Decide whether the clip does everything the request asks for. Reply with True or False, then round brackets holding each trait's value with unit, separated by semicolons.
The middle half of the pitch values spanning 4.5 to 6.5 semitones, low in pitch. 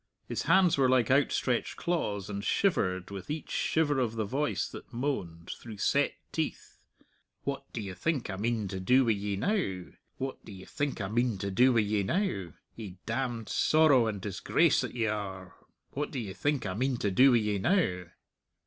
True (5.6 semitones; 115 Hz)